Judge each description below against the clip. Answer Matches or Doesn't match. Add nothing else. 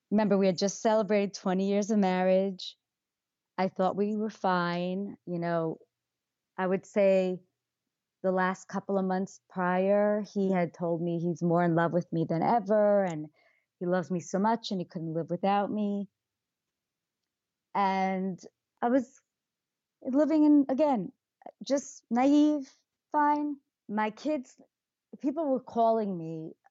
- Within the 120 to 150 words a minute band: Matches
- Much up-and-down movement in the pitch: Doesn't match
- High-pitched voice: Matches